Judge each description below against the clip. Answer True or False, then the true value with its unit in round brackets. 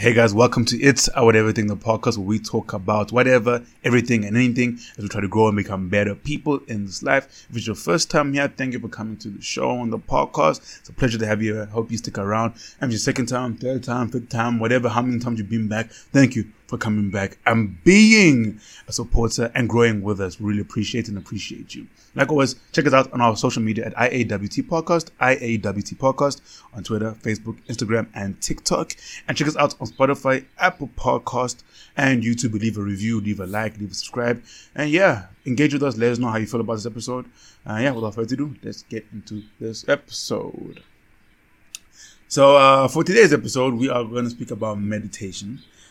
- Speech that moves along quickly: True (220 wpm)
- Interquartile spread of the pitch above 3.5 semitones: False (3.0 semitones)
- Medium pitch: False (115 Hz)